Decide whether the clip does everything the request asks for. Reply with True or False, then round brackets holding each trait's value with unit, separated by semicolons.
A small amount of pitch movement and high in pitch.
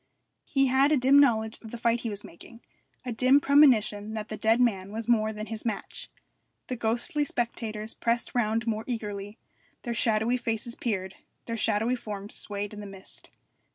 True (2.3 semitones; 225 Hz)